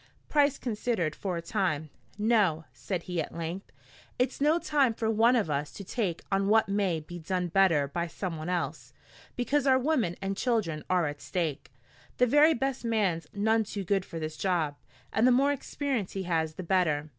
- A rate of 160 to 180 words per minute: No, average, 190 wpm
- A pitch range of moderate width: No, wide, 5.8 semitones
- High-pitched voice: Yes, high, 195 Hz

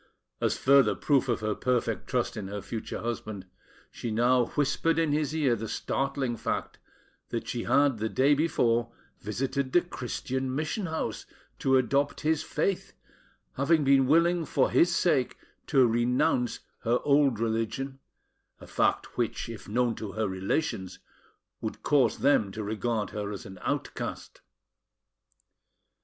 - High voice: No, low, 130 Hz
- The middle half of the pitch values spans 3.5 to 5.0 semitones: Yes, average, 4.3 semitones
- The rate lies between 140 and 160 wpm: Yes, average, 145 wpm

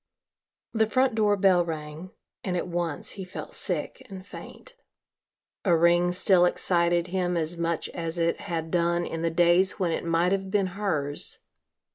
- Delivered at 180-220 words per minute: No, average, 165 wpm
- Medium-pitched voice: Yes, medium, 175 Hz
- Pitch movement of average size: No, narrow, 2.0 semitones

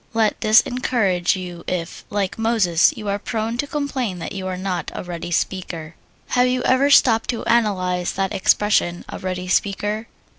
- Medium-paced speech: Yes, average, 175 wpm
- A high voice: Yes, high, 200 Hz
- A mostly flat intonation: No, average, 4.1 semitones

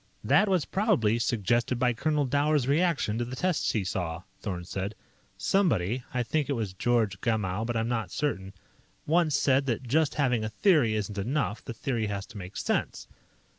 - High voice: No, low, 120 Hz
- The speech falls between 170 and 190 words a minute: Yes, average, 180 wpm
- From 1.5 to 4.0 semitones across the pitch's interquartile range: No, wide, 5.5 semitones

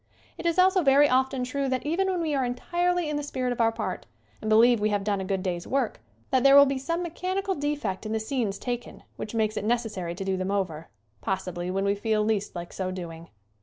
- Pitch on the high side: Yes, high, 235 Hz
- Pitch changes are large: Yes, wide, 6.4 semitones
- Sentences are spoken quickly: Yes, fast, 240 wpm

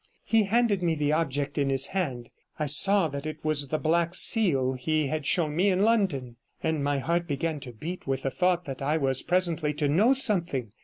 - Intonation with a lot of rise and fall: No, average, 4.4 semitones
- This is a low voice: No, medium, 155 Hz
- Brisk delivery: Yes, fast, 210 wpm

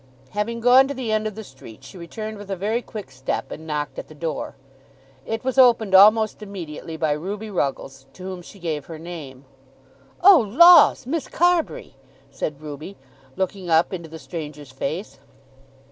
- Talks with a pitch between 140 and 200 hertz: Yes, medium, 185 Hz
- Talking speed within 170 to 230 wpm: Yes, average, 175 wpm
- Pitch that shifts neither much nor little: No, wide, 6.2 semitones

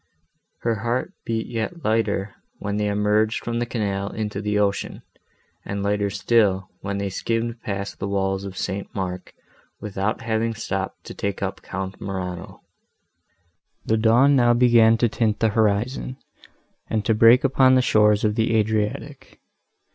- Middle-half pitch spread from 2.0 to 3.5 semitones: Yes, narrow, 2.4 semitones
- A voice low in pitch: Yes, low, 105 Hz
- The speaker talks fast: No, average, 155 wpm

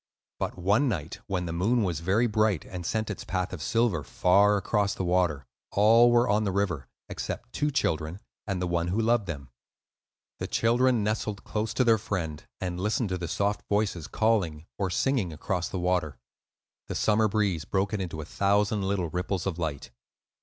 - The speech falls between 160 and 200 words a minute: Yes, average, 185 wpm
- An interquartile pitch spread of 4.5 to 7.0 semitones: No, average, 3.6 semitones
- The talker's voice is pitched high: No, very low, 95 Hz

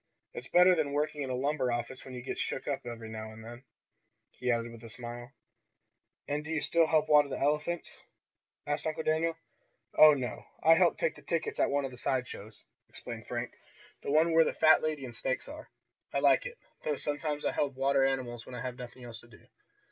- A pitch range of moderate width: Yes, average, 4.1 semitones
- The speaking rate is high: Yes, fast, 220 wpm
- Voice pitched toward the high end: No, medium, 140 Hz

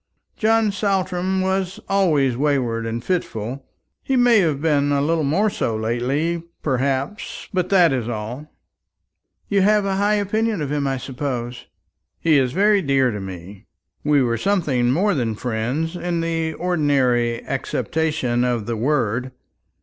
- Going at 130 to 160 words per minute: Yes, average, 150 wpm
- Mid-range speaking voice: Yes, medium, 145 Hz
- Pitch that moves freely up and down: Yes, wide, 7.0 semitones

